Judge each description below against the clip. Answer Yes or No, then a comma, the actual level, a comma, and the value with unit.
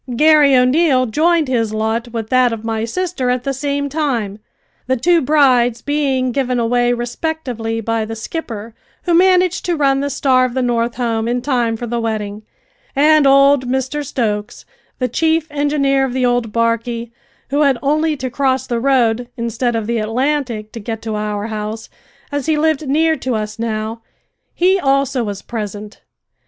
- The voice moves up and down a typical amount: Yes, average, 3.9 semitones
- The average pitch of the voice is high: Yes, very high, 250 Hz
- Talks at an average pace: Yes, average, 175 wpm